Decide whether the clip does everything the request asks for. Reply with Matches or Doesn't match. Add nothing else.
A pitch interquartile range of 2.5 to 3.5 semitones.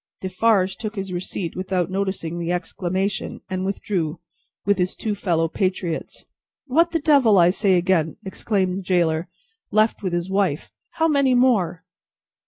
Matches